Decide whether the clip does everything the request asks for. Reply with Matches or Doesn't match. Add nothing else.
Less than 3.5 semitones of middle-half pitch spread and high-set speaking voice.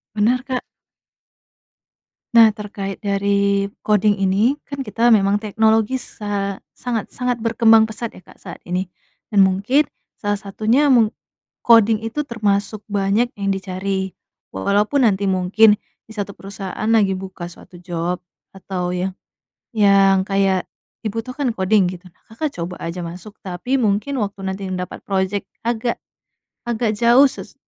Matches